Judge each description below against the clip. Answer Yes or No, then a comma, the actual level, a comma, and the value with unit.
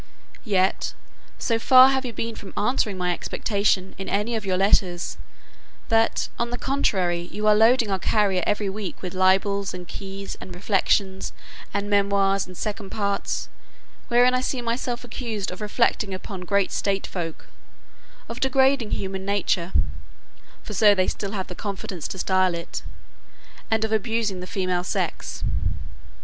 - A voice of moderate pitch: No, high, 200 Hz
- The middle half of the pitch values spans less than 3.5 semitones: Yes, average, 3.0 semitones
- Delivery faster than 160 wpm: No, average, 155 wpm